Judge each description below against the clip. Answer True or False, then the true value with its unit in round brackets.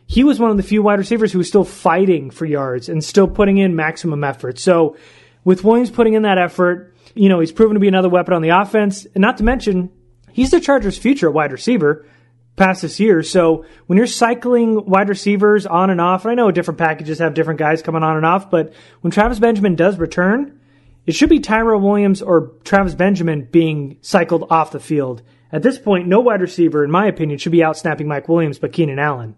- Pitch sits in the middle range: True (180 Hz)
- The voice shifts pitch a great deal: False (4.6 semitones)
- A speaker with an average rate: False (225 wpm)